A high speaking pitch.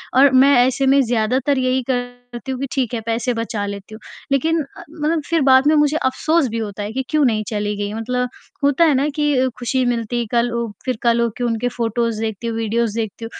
Yes: high, 245 Hz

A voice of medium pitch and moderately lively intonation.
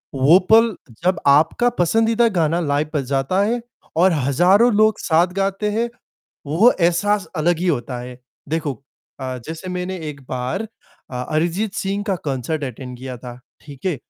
No: medium, 165 Hz; wide, 6.0 semitones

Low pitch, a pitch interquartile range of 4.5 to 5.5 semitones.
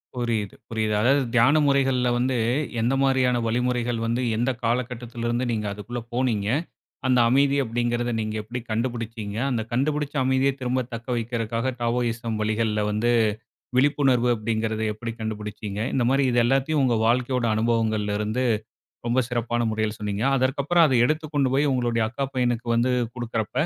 No: low, 120 Hz; narrow, 2.4 semitones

